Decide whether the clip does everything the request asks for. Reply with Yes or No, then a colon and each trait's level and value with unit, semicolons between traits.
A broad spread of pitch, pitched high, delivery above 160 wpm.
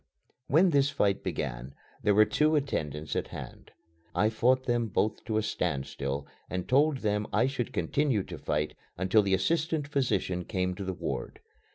No: wide, 7.0 semitones; low, 110 Hz; average, 170 wpm